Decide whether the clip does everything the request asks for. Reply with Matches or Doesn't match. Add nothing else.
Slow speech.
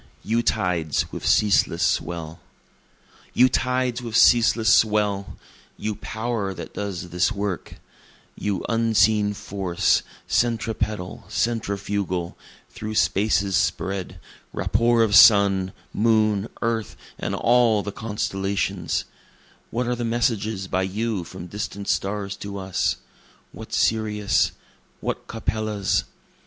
Matches